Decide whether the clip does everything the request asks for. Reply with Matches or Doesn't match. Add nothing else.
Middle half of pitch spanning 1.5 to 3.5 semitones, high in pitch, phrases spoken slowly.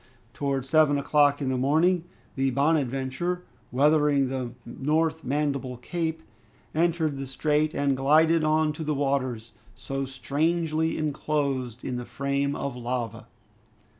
Doesn't match